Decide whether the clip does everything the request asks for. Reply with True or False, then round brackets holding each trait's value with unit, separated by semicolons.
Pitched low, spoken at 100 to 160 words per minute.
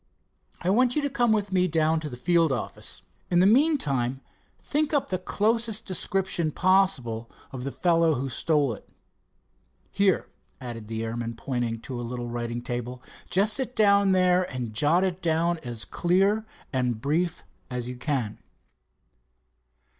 False (160 Hz; 155 wpm)